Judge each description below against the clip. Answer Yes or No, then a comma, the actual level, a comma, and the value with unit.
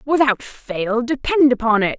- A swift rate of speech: No, average, 150 wpm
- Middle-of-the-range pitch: No, very high, 250 Hz